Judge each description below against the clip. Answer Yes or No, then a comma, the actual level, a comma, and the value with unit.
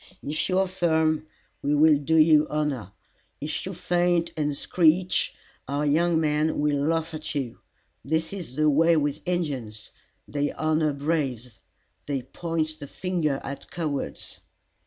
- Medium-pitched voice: Yes, medium, 155 Hz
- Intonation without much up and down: Yes, narrow, 2.3 semitones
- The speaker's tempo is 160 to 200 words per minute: No, average, 145 wpm